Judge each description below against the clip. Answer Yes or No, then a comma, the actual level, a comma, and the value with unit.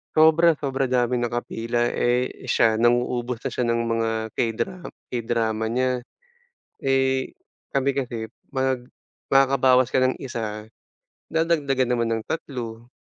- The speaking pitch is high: No, low, 125 Hz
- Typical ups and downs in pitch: No, narrow, 2.2 semitones